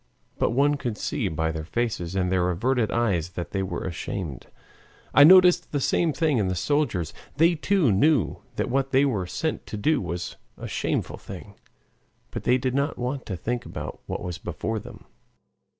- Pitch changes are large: Yes, wide, 7.8 semitones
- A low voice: Yes, low, 120 Hz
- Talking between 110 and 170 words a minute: No, average, 185 wpm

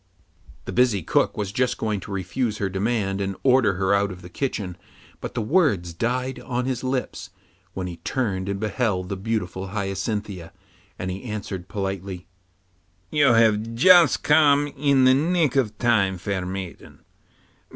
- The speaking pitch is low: Yes, low, 105 Hz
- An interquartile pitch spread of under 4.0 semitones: No, average, 4.9 semitones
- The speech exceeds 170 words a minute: No, average, 160 wpm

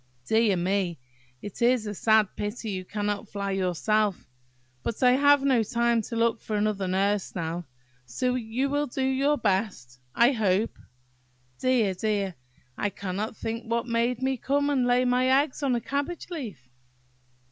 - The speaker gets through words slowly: No, average, 160 wpm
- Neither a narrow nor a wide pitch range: Yes, average, 4.1 semitones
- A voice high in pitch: Yes, high, 225 Hz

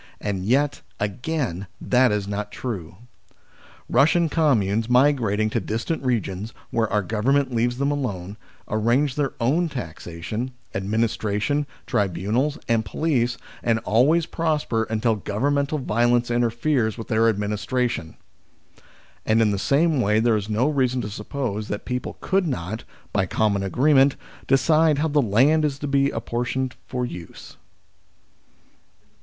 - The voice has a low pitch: Yes, low, 120 Hz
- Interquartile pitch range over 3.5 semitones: Yes, average, 4.9 semitones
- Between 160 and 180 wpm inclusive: No, slow, 135 wpm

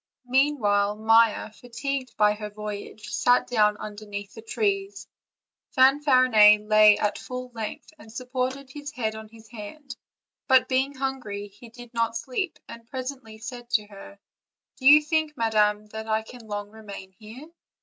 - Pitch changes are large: No, average, 3.7 semitones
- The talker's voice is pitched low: No, high, 230 Hz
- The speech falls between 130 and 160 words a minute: Yes, average, 155 wpm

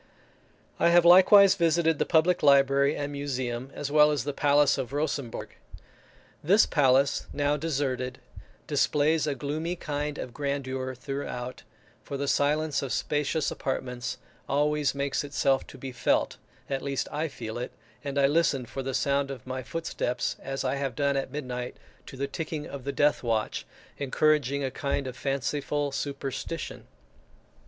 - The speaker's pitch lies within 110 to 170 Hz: Yes, medium, 140 Hz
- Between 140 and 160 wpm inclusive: Yes, average, 155 wpm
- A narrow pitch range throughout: Yes, narrow, 2.0 semitones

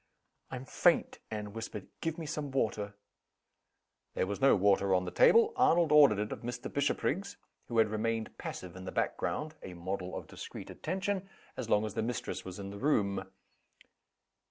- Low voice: Yes, low, 110 Hz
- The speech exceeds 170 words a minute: Yes, average, 180 wpm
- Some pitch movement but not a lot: No, wide, 7.0 semitones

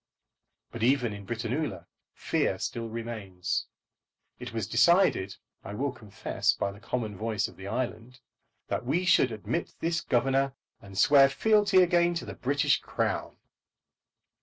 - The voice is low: Yes, low, 120 Hz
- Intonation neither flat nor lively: Yes, average, 4.9 semitones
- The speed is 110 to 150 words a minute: Yes, average, 140 wpm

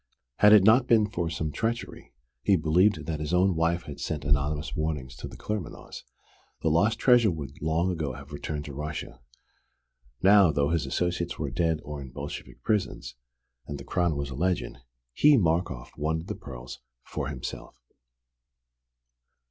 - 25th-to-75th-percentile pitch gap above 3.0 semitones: Yes, average, 4.2 semitones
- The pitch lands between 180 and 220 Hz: No, very low, 80 Hz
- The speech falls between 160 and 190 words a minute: Yes, average, 165 wpm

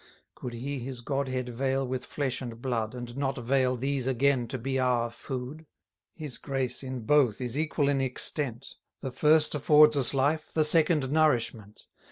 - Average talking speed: Yes, average, 170 wpm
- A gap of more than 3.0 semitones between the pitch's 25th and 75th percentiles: No, narrow, 2.5 semitones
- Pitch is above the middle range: No, low, 130 Hz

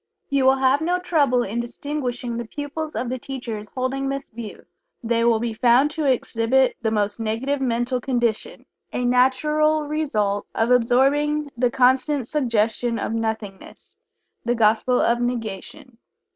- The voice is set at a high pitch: Yes, very high, 250 Hz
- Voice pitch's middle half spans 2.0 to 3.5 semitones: Yes, average, 3.2 semitones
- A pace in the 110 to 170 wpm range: Yes, average, 145 wpm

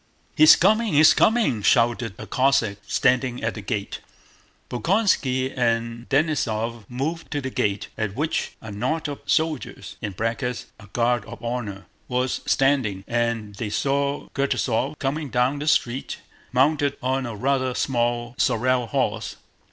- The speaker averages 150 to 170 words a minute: No, slow, 135 wpm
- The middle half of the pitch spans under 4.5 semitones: Yes, average, 3.4 semitones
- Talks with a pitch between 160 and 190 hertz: No, low, 125 Hz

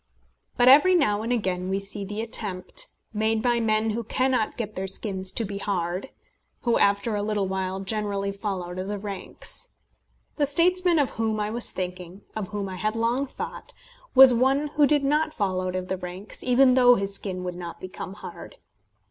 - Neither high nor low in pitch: No, high, 210 Hz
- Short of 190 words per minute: No, average, 195 wpm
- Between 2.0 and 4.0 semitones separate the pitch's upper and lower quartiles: No, average, 4.4 semitones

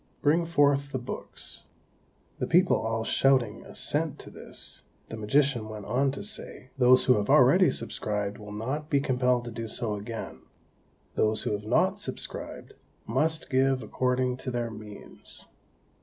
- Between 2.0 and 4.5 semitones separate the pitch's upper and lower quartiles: Yes, average, 4.1 semitones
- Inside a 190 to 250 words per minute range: No, average, 155 wpm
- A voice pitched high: No, low, 125 Hz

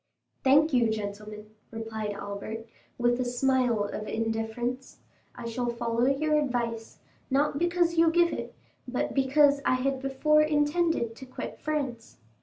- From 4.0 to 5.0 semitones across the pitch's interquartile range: Yes, average, 4.5 semitones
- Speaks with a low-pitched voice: No, very high, 250 Hz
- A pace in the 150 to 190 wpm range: No, slow, 135 wpm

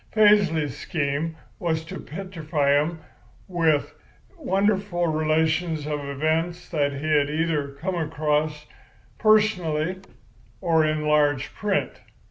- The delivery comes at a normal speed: No, slow, 105 wpm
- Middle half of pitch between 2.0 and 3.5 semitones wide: Yes, average, 2.7 semitones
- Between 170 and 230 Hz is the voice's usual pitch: No, medium, 160 Hz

